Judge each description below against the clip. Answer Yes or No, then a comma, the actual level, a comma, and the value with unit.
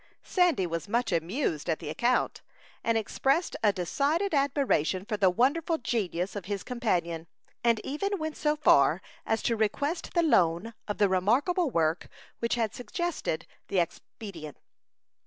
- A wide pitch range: Yes, wide, 8.0 semitones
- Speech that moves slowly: No, average, 150 wpm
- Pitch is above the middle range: Yes, high, 225 Hz